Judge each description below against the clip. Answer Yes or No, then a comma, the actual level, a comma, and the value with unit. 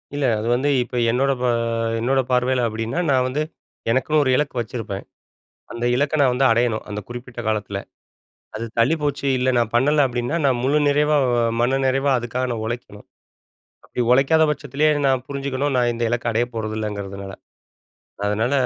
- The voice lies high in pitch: No, low, 125 Hz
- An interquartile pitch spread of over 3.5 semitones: No, average, 3.2 semitones